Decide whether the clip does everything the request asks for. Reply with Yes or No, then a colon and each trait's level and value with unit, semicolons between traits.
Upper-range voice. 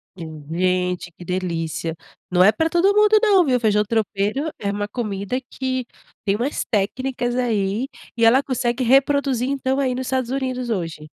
Yes: high, 235 Hz